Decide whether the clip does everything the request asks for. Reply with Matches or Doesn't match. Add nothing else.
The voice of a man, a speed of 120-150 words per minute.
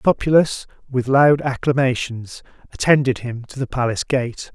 Matches